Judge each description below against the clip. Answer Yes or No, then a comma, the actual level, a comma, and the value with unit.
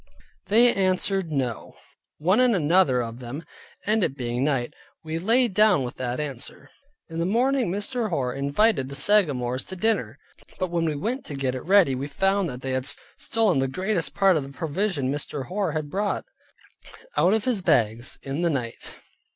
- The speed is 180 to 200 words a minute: Yes, average, 185 wpm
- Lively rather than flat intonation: Yes, wide, 7.0 semitones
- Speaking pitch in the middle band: Yes, medium, 165 Hz